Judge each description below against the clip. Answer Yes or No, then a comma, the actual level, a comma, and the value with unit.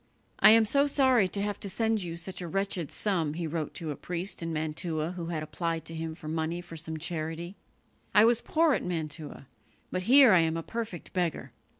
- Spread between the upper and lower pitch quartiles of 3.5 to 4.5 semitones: Yes, average, 3.8 semitones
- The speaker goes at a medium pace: No, fast, 215 wpm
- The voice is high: No, medium, 175 Hz